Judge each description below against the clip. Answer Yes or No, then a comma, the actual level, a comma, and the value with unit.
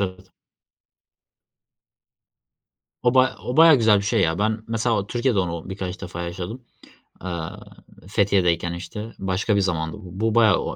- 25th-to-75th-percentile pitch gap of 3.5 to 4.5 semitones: Yes, average, 3.8 semitones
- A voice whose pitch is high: No, low, 100 Hz